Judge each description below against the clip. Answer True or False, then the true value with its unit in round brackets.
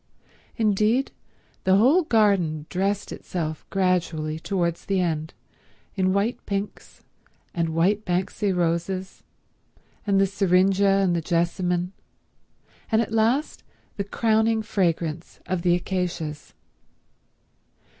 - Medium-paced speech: False (105 wpm)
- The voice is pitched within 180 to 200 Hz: True (185 Hz)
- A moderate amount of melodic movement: True (3.0 semitones)